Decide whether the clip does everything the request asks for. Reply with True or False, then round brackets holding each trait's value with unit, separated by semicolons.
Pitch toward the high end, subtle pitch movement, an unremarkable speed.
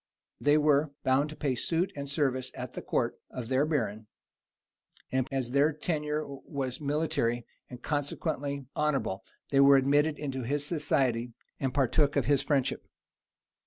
False (140 Hz; 2.3 semitones; 150 wpm)